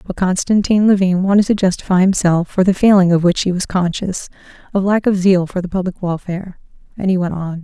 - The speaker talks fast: Yes, fast, 210 wpm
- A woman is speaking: Yes, female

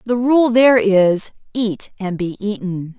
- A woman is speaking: Yes, female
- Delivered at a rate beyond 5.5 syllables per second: No, 4.0 syllables/s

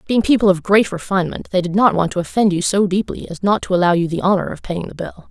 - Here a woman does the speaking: Yes, female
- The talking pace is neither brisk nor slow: No, fast, 285 wpm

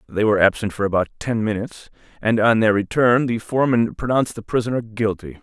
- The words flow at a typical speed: Yes, average, 190 wpm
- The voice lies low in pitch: Yes, low, 110 Hz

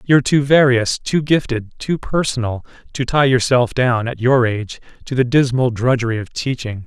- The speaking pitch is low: Yes, low, 125 Hz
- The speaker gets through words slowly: No, average, 175 wpm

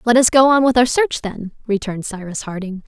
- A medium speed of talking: No, fast, 230 wpm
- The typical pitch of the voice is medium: No, high, 225 Hz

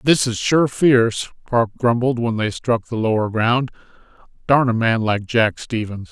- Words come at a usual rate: Yes, average, 175 wpm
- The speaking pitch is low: Yes, low, 120 Hz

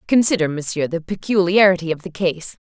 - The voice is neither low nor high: Yes, medium, 180 Hz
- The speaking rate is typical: Yes, average, 155 wpm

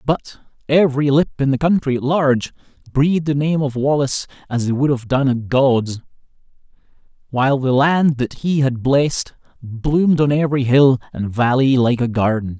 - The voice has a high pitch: No, low, 135 Hz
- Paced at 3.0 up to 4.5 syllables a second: No, 5.1 syllables/s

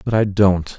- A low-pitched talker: Yes, low, 100 Hz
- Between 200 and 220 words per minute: No, fast, 230 wpm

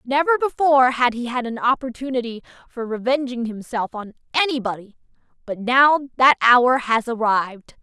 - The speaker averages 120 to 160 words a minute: Yes, average, 140 wpm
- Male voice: No, female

